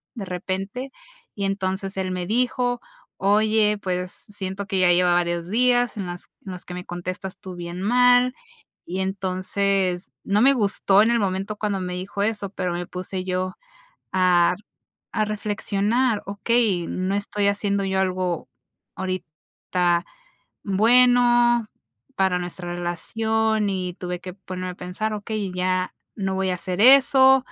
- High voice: Yes, high, 195 Hz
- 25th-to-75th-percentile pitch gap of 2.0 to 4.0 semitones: Yes, average, 2.8 semitones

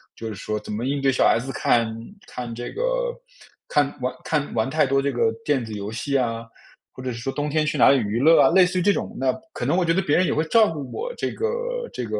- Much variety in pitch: Yes, wide, 6.1 semitones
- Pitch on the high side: No, low, 135 Hz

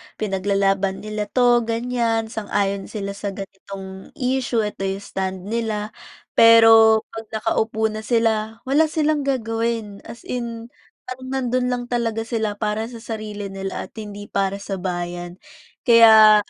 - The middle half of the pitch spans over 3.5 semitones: No, average, 2.8 semitones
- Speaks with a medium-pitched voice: No, high, 220 Hz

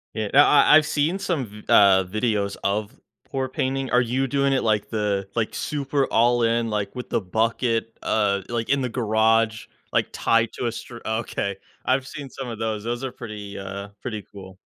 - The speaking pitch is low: Yes, low, 115 Hz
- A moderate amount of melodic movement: Yes, average, 3.7 semitones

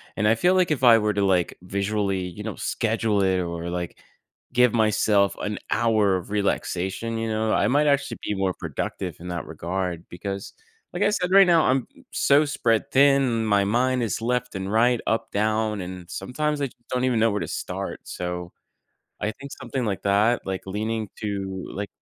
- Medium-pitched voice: No, low, 105 Hz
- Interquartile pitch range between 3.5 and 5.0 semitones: Yes, average, 4.2 semitones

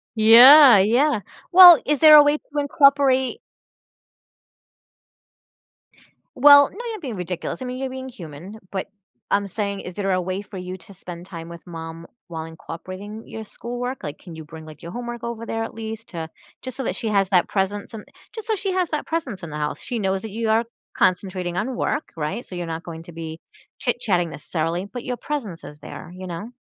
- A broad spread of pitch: Yes, wide, 6.6 semitones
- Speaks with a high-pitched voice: Yes, high, 205 Hz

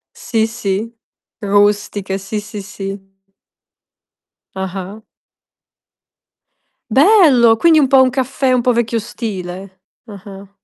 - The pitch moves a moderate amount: Yes, average, 3.8 semitones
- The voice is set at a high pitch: Yes, high, 210 Hz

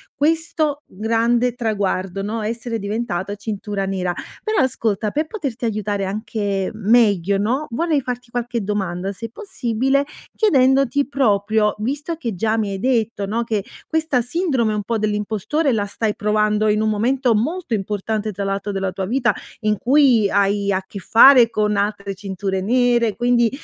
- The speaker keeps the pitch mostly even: No, average, 3.6 semitones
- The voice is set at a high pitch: Yes, high, 220 Hz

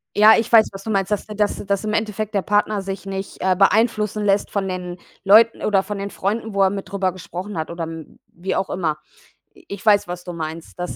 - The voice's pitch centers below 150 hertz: No, high, 195 Hz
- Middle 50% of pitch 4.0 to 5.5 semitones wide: No, narrow, 2.4 semitones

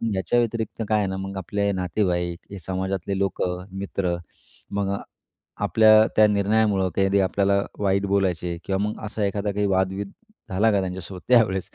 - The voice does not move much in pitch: Yes, narrow, 1.6 semitones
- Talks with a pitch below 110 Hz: Yes, low, 100 Hz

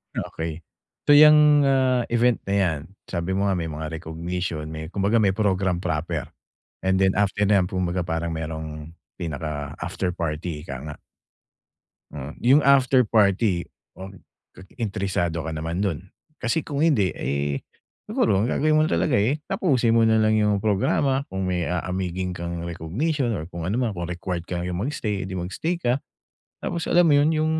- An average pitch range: No, wide, 5.8 semitones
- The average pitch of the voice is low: Yes, very low, 95 Hz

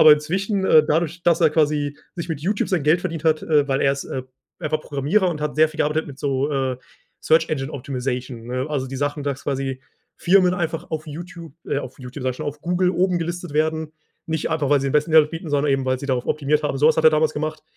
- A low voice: No, medium, 150 Hz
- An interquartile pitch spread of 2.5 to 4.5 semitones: Yes, average, 2.8 semitones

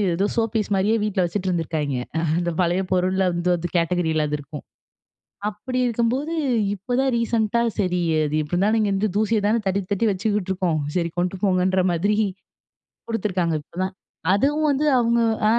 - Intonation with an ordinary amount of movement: Yes, average, 4.0 semitones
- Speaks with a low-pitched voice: No, high, 190 Hz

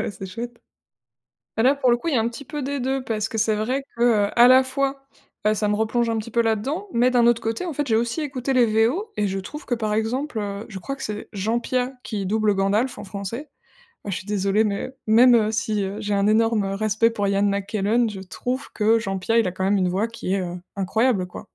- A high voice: Yes, high, 225 Hz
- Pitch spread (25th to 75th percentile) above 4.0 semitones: No, average, 3.6 semitones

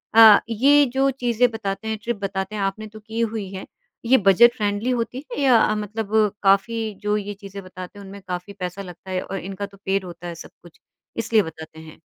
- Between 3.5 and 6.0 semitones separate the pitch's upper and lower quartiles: No, average, 2.9 semitones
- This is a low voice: No, high, 205 Hz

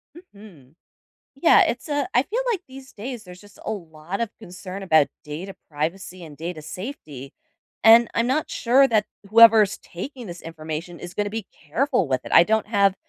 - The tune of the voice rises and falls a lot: Yes, wide, 5.8 semitones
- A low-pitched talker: No, high, 200 Hz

